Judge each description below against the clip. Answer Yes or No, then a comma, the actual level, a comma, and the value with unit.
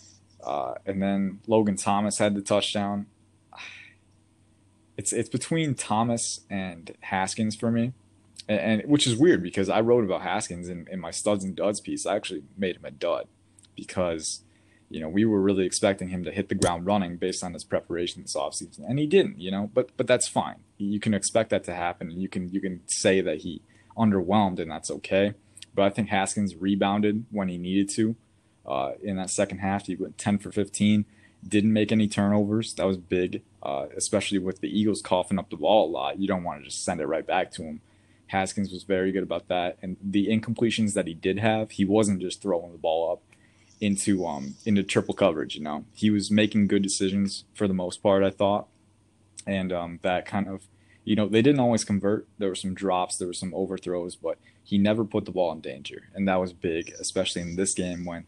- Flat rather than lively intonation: Yes, narrow, 2.1 semitones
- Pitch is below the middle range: Yes, low, 100 Hz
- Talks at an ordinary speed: No, fast, 210 wpm